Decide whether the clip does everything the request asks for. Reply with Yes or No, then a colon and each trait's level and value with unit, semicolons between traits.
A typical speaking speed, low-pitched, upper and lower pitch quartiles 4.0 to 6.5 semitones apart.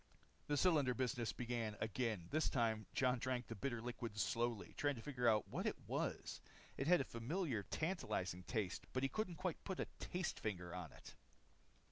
Yes: average, 180 wpm; low, 120 Hz; average, 4.7 semitones